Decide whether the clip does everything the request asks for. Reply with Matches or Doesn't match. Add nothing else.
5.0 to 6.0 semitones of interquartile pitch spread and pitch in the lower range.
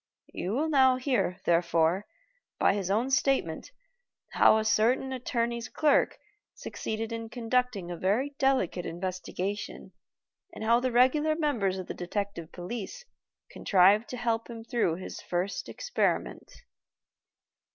Doesn't match